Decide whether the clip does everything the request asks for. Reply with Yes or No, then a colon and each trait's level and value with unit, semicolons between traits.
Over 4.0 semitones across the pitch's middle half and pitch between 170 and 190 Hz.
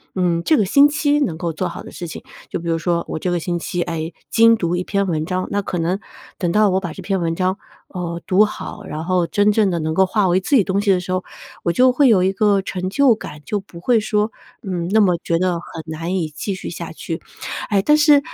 No: average, 3.5 semitones; medium, 185 Hz